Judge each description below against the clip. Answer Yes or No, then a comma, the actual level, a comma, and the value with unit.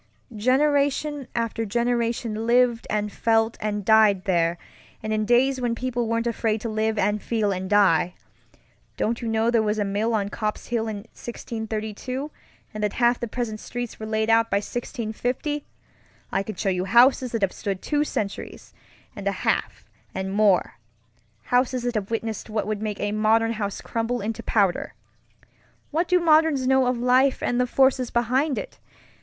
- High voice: Yes, high, 225 Hz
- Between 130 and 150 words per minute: No, average, 170 wpm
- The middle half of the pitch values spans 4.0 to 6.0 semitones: No, average, 2.7 semitones